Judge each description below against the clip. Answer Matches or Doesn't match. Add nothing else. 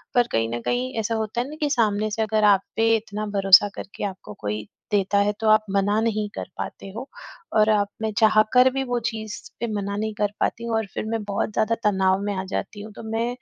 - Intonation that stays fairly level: Matches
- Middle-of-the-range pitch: Doesn't match